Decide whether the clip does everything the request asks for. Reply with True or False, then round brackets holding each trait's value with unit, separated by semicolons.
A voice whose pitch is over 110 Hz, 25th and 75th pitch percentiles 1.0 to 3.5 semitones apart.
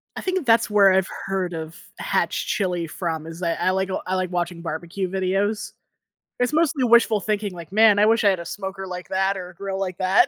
True (190 Hz; 2.7 semitones)